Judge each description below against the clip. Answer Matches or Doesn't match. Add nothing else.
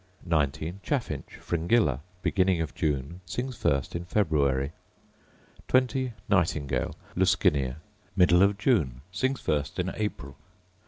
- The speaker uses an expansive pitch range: Matches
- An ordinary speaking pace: Doesn't match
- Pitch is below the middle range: Matches